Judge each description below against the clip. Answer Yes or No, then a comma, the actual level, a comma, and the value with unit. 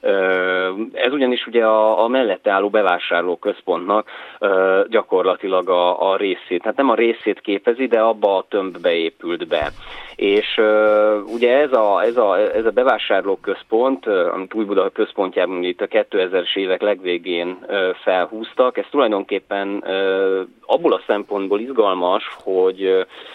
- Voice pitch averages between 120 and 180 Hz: No, low, 110 Hz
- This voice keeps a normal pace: Yes, average, 145 wpm